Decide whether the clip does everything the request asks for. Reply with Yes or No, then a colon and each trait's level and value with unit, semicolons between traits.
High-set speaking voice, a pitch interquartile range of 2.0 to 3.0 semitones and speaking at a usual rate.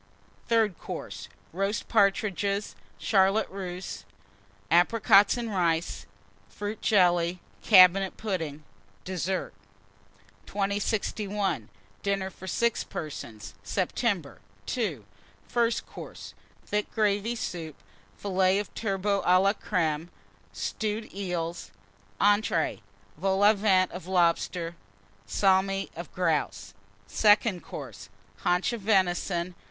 No: high, 195 Hz; average, 2.7 semitones; slow, 95 wpm